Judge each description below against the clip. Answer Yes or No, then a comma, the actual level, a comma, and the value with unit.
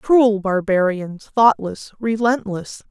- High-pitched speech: Yes, high, 210 Hz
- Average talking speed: No, slow, 85 wpm